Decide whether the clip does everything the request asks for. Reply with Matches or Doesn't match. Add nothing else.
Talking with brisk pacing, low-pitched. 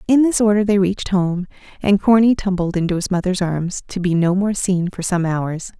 Doesn't match